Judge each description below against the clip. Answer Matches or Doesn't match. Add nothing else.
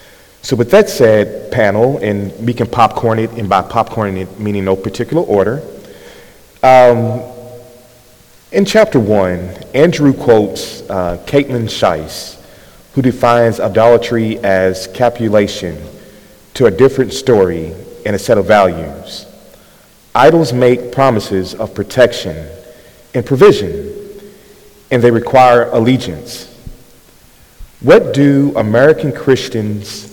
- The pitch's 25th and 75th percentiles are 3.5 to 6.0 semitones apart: Matches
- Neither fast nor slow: Doesn't match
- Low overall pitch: Matches